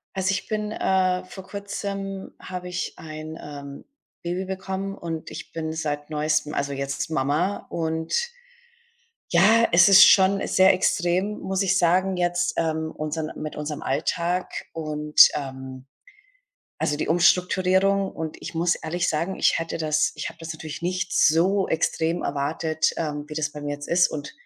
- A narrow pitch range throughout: No, average, 3.5 semitones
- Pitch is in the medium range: Yes, medium, 165 Hz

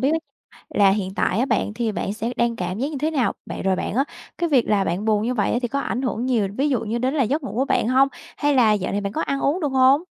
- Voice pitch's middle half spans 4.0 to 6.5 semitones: Yes, average, 4.5 semitones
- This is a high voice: Yes, high, 240 Hz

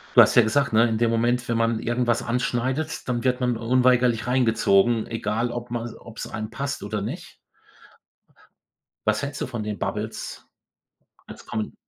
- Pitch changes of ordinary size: No, narrow, 1.9 semitones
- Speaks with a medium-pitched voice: No, low, 120 Hz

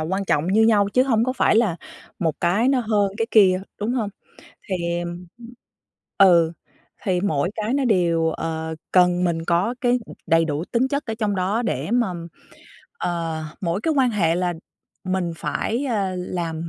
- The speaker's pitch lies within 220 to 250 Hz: No, high, 190 Hz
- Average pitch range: Yes, average, 4.9 semitones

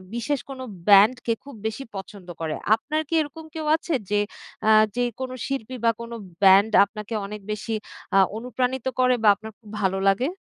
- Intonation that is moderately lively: Yes, average, 4.0 semitones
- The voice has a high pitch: Yes, high, 230 Hz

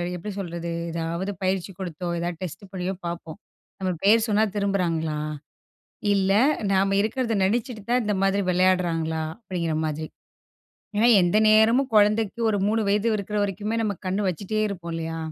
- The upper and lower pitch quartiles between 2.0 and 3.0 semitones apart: No, average, 3.6 semitones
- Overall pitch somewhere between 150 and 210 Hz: Yes, high, 190 Hz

